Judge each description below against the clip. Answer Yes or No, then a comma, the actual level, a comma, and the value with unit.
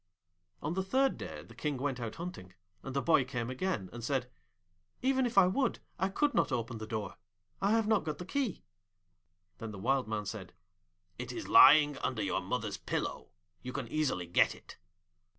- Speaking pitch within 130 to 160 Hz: Yes, medium, 140 Hz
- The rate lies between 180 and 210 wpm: Yes, average, 190 wpm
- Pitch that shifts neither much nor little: No, wide, 8.4 semitones